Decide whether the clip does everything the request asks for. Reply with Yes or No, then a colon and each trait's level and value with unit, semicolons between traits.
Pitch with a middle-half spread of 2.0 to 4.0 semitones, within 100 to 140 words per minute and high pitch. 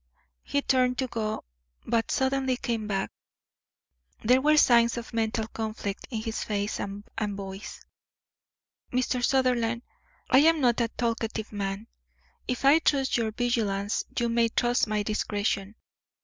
Yes: average, 2.9 semitones; slow, 135 wpm; high, 230 Hz